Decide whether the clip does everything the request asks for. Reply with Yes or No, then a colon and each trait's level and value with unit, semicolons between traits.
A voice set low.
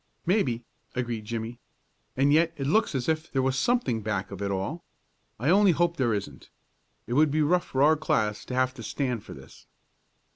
Yes: low, 130 Hz